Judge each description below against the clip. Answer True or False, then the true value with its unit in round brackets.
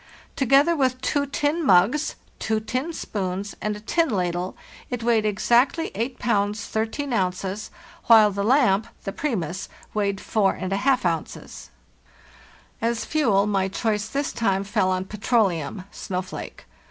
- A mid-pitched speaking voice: False (215 Hz)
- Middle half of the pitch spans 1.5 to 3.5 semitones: False (4.6 semitones)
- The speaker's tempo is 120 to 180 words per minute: True (140 wpm)